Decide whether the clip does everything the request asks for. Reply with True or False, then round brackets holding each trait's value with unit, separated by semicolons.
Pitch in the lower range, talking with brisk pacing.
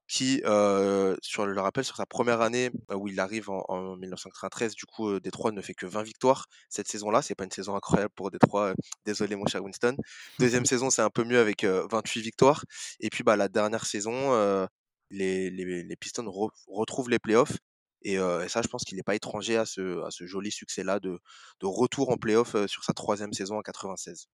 True (105 Hz; 225 wpm)